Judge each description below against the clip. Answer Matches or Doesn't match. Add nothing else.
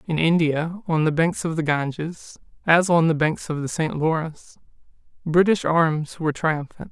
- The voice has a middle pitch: Matches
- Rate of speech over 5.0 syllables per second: Doesn't match